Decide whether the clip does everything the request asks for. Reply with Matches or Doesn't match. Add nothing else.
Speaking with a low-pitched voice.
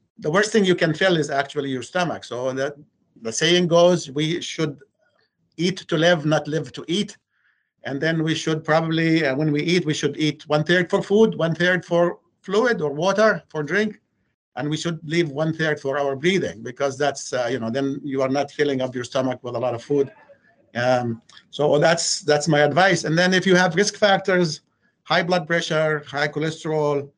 Doesn't match